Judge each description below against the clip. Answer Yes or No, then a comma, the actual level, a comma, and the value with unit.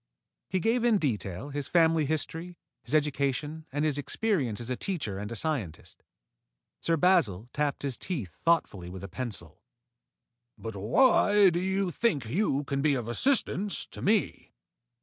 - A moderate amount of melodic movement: No, wide, 7.3 semitones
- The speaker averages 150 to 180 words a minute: Yes, average, 155 wpm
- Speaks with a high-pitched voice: No, medium, 145 Hz